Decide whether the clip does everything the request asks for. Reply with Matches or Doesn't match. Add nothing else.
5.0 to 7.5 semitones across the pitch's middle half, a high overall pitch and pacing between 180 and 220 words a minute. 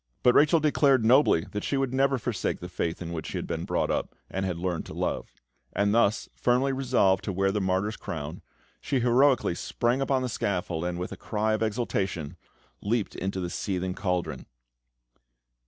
Doesn't match